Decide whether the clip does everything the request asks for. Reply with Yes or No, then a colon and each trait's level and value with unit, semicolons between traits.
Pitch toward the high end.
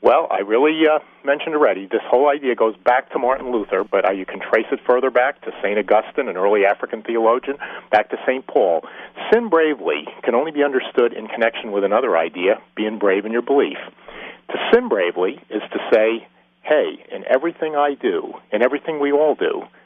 No: medium, 140 Hz